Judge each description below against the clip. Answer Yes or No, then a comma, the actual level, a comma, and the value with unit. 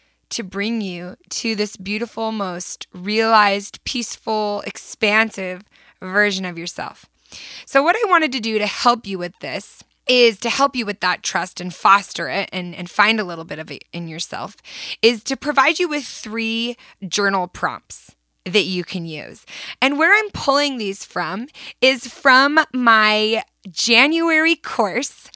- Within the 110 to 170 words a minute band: Yes, average, 160 wpm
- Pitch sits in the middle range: No, high, 215 Hz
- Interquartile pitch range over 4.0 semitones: Yes, average, 4.6 semitones